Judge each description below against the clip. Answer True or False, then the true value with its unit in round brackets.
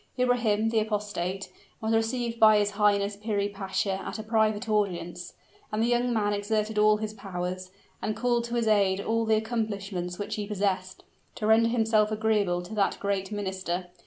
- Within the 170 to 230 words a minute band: True (175 wpm)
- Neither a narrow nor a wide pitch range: False (2.1 semitones)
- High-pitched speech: True (210 Hz)